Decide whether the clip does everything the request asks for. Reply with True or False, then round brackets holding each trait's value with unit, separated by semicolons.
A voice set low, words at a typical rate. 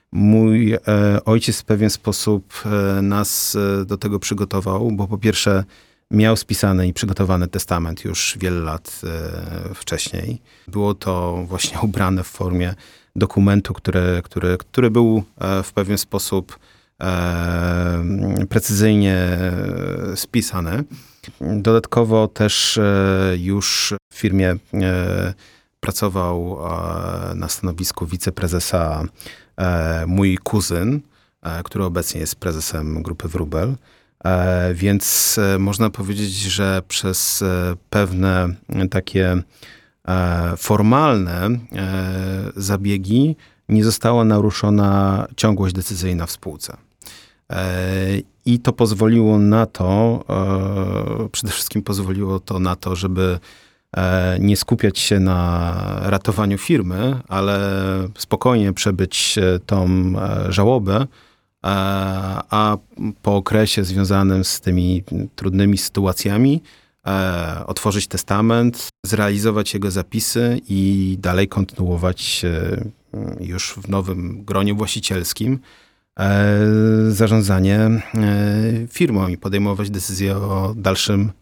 False (100 Hz; 90 wpm)